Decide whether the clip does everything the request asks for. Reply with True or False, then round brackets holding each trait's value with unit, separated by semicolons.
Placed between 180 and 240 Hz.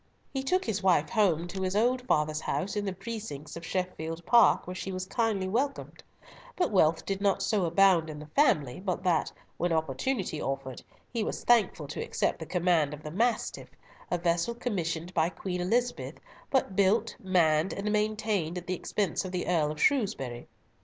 True (185 Hz)